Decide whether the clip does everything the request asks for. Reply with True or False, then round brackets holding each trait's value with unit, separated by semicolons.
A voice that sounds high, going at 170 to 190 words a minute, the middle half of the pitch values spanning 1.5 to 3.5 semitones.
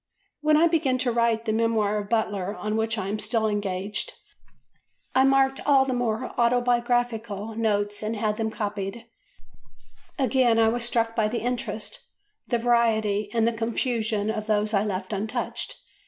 False (225 Hz; 160 wpm; 2.4 semitones)